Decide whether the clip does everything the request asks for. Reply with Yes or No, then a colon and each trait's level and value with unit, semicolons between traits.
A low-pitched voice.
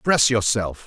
Yes: low, 115 Hz